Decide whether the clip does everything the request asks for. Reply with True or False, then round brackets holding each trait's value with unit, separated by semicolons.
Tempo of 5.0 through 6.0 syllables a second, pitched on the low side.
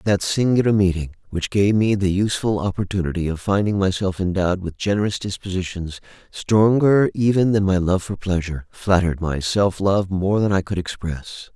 True (5.4 syllables/s; 95 Hz)